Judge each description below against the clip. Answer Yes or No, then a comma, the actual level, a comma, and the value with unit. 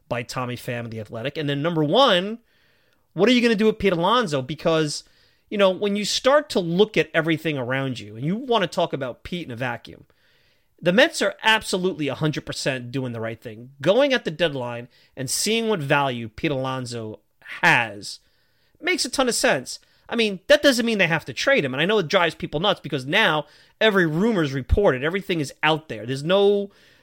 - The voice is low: No, medium, 165 Hz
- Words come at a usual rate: No, fast, 210 wpm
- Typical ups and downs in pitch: No, wide, 7.5 semitones